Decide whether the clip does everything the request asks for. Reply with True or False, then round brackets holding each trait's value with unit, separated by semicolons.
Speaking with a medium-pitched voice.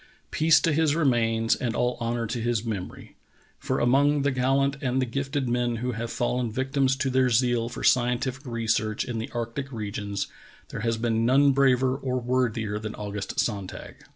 False (120 Hz)